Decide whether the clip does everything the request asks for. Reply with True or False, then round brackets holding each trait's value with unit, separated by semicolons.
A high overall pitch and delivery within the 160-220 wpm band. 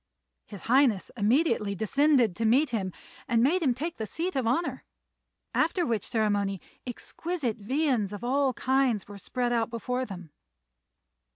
False (240 Hz; 150 wpm)